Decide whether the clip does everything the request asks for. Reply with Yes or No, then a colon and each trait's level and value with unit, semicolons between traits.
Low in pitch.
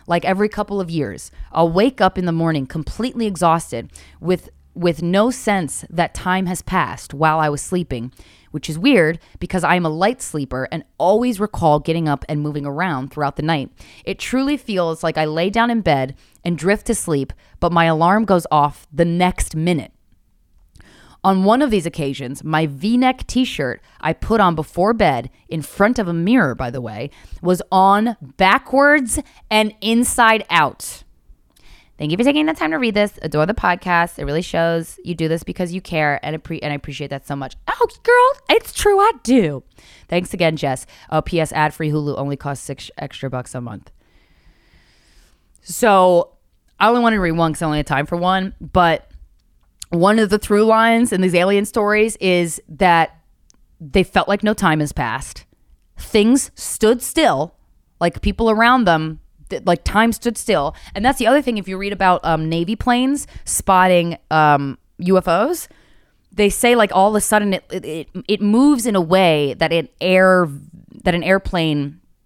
No: medium, 175 Hz